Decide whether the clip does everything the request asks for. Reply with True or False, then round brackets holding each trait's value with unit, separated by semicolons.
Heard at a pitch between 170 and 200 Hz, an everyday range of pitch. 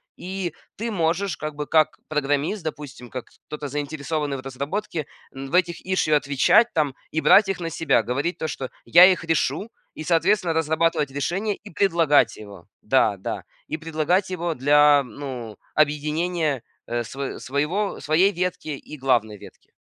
False (155 Hz; 3.8 semitones)